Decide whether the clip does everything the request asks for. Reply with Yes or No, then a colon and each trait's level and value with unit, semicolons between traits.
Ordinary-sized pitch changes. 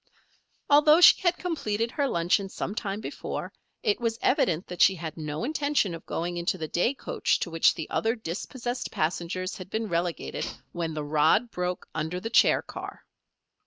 No: wide, 5.8 semitones